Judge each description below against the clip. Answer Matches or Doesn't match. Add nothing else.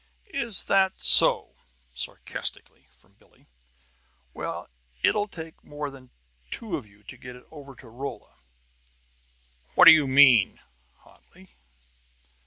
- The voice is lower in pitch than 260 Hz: Matches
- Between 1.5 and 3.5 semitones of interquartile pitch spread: Doesn't match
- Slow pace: Matches